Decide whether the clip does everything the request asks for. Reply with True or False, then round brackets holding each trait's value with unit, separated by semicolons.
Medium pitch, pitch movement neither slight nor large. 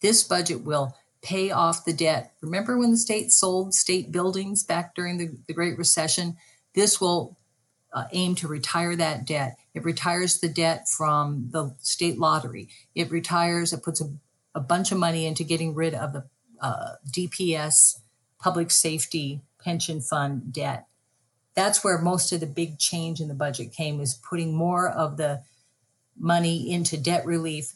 True (165 Hz; 3.0 semitones)